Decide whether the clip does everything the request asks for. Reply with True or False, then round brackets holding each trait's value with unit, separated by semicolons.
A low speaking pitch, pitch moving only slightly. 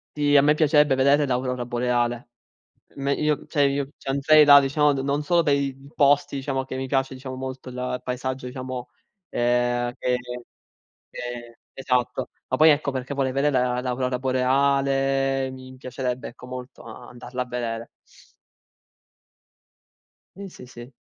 True (130 Hz; 2.0 semitones)